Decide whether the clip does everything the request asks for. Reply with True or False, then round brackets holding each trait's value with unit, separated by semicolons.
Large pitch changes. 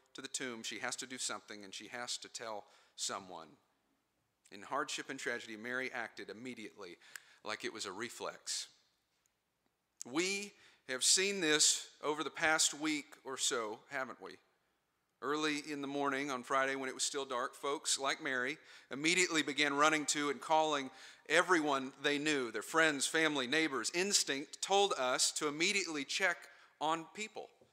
False (3.2 semitones)